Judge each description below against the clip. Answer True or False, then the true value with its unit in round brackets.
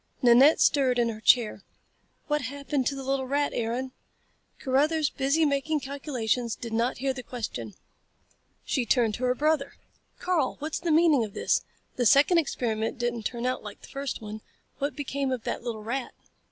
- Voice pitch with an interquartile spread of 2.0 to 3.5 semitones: True (3.2 semitones)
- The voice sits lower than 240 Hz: False (260 Hz)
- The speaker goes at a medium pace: True (175 wpm)